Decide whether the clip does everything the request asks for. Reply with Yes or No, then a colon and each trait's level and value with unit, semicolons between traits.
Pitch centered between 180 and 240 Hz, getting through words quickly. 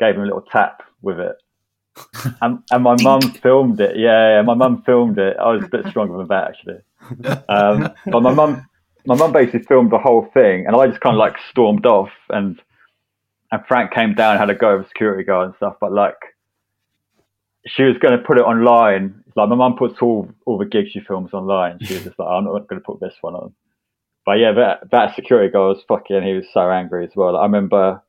No: low, 115 Hz; fast, 235 wpm